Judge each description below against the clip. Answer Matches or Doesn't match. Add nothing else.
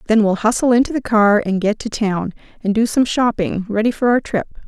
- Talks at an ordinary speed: Doesn't match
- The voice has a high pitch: Matches